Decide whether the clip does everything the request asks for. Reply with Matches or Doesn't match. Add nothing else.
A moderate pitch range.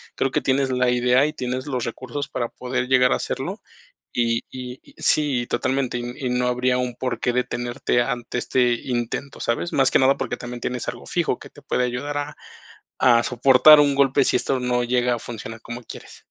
Doesn't match